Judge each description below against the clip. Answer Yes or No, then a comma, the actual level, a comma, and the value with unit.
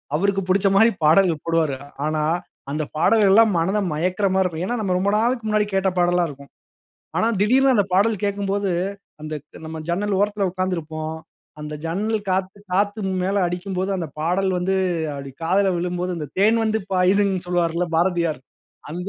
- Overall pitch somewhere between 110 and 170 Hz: No, medium, 185 Hz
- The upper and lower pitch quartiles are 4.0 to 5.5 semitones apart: No, average, 3.3 semitones